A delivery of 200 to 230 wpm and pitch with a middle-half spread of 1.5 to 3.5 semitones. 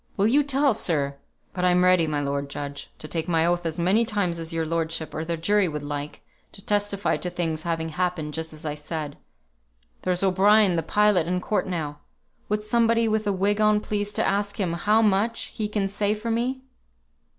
No: fast, 205 wpm; average, 4.5 semitones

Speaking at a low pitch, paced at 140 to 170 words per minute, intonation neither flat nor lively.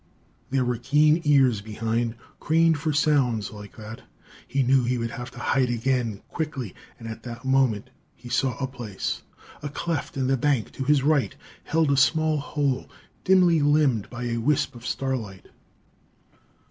Yes: low, 130 Hz; average, 165 wpm; average, 3.8 semitones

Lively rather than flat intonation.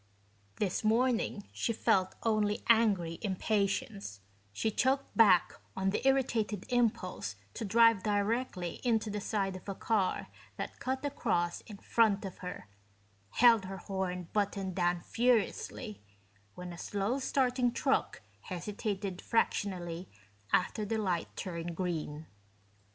No: average, 3.8 semitones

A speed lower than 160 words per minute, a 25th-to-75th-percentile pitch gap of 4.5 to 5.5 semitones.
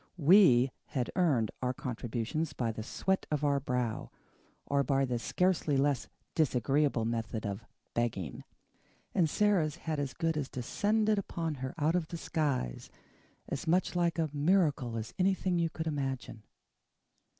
Yes: average, 150 wpm; average, 5.2 semitones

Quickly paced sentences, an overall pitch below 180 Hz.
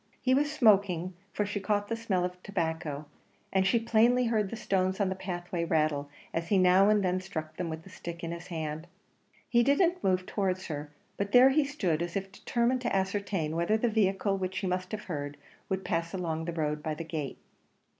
No: fast, 215 wpm; medium, 185 Hz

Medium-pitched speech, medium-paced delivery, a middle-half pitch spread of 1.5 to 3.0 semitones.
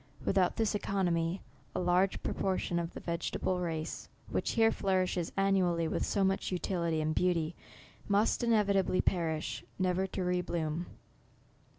Yes: medium, 180 Hz; average, 150 wpm; narrow, 2.4 semitones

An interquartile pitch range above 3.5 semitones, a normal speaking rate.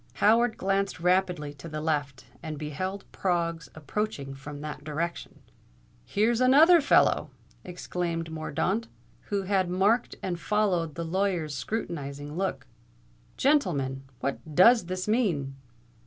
No: average, 5.0 semitones; slow, 120 wpm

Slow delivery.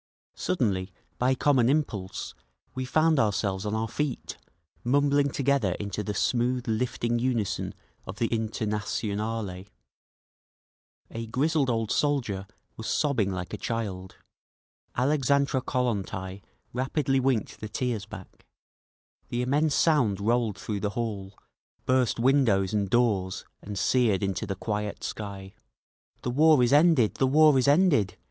Yes: slow, 130 wpm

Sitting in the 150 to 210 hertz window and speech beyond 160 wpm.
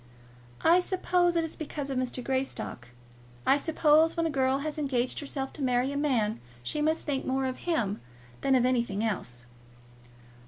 No: very high, 270 Hz; average, 170 wpm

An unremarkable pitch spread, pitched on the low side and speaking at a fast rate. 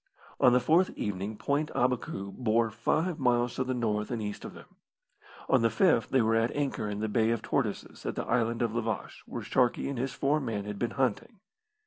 Yes: average, 3.0 semitones; low, 120 Hz; fast, 220 wpm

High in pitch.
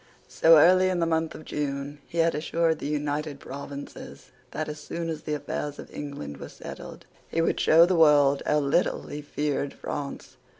No: medium, 150 Hz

